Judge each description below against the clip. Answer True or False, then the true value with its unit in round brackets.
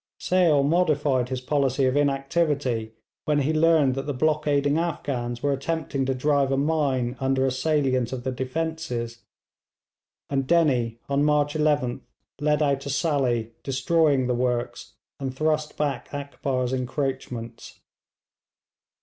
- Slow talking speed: True (130 wpm)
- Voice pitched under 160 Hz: True (140 Hz)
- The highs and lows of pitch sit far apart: False (2.8 semitones)